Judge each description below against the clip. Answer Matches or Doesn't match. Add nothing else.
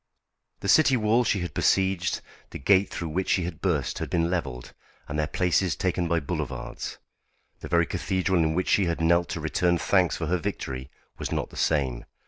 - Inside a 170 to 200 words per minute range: Matches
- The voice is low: Matches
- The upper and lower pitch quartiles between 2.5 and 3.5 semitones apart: Matches